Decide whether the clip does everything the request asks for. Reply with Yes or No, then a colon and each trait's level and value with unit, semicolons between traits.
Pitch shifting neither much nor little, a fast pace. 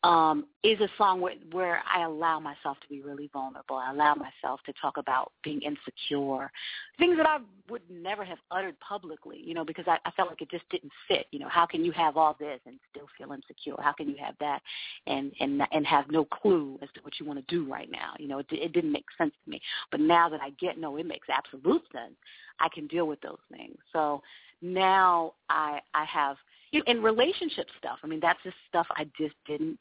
Yes: average, 4.1 semitones; fast, 230 wpm